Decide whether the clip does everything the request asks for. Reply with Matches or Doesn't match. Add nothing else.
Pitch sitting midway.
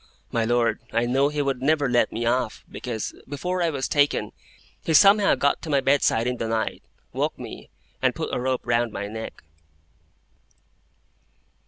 Doesn't match